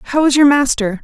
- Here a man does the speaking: No, female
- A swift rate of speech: Yes, fast, 230 wpm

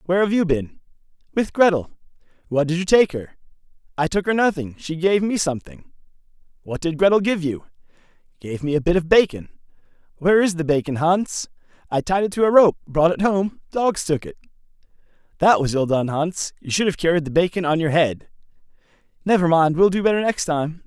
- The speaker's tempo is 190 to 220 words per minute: Yes, average, 195 wpm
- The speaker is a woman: No, male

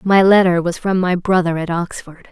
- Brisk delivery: Yes, fast, 210 wpm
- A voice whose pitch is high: No, medium, 180 Hz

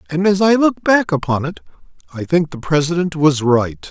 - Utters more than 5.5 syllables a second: No, 5.0 syllables/s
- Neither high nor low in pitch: Yes, medium, 165 Hz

